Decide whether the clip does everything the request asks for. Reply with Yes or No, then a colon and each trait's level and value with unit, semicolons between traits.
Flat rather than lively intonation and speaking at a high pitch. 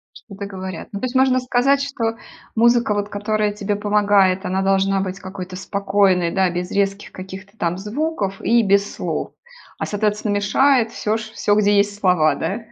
Yes: narrow, 2.3 semitones; high, 205 Hz